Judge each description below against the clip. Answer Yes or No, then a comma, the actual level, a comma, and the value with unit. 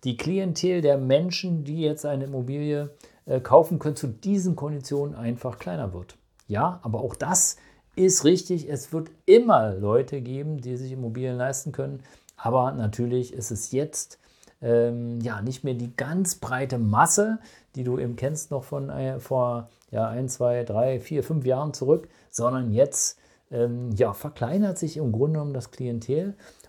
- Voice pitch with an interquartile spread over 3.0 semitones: Yes, average, 3.8 semitones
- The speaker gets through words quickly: No, average, 160 wpm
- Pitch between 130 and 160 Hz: Yes, low, 135 Hz